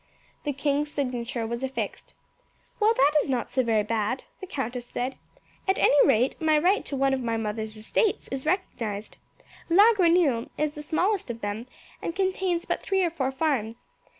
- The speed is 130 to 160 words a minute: No, average, 180 wpm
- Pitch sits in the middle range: No, very high, 270 Hz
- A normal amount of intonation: No, wide, 6.2 semitones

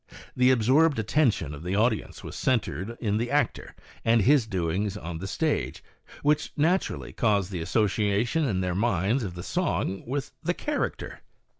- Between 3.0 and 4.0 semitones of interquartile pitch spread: No, wide, 5.6 semitones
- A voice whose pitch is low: Yes, low, 110 Hz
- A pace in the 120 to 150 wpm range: No, average, 160 wpm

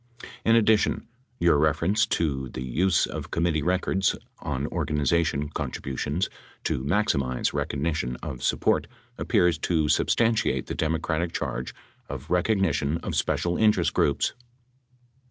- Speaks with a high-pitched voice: No, very low, 80 Hz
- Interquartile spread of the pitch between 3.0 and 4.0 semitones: No, average, 4.4 semitones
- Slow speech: Yes, slow, 125 wpm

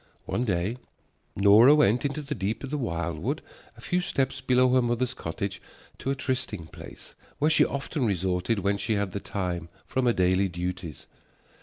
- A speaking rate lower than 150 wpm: No, average, 175 wpm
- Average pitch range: No, wide, 6.0 semitones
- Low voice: Yes, low, 110 Hz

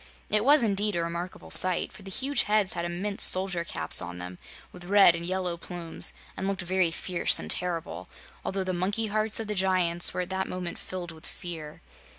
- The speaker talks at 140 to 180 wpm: No, average, 200 wpm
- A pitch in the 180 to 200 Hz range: Yes, medium, 185 Hz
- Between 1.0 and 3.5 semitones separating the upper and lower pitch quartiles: Yes, narrow, 2.5 semitones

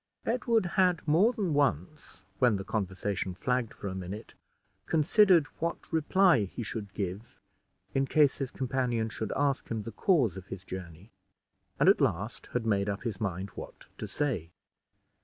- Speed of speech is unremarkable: Yes, average, 160 wpm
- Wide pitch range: Yes, wide, 7.3 semitones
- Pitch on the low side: Yes, low, 115 Hz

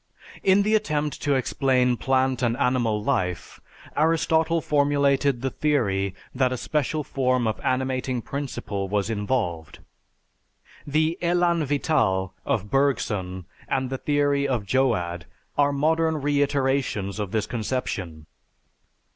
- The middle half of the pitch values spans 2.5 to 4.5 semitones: No, average, 5.1 semitones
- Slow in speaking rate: Yes, slow, 120 wpm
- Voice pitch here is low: Yes, low, 130 Hz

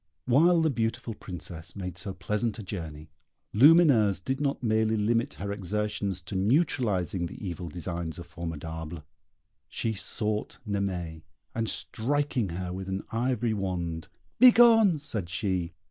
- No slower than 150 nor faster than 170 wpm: No, slow, 135 wpm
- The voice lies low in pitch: Yes, low, 100 Hz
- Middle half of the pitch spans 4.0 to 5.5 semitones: Yes, average, 5.0 semitones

